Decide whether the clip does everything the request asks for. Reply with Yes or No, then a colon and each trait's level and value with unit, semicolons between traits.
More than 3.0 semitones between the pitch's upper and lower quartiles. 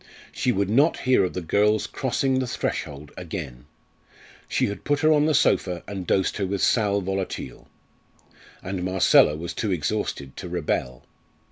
Yes: average, 4.4 semitones